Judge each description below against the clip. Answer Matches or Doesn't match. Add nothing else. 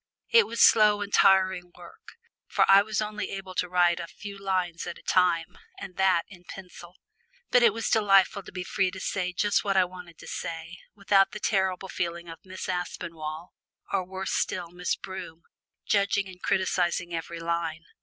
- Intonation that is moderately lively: Doesn't match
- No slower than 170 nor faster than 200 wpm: Matches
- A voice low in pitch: Doesn't match